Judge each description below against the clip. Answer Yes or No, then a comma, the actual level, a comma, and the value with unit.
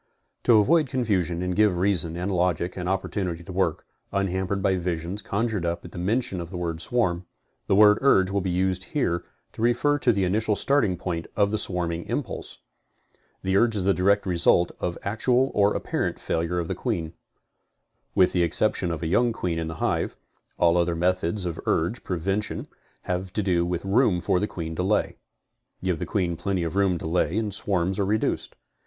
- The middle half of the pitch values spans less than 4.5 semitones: Yes, average, 2.9 semitones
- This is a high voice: No, very low, 95 Hz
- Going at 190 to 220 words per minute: Yes, average, 195 wpm